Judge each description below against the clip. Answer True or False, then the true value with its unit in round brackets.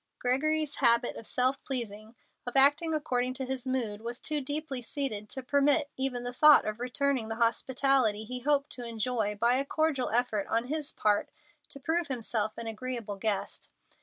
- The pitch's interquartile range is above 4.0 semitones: False (3.5 semitones)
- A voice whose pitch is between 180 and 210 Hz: False (250 Hz)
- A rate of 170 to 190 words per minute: True (175 wpm)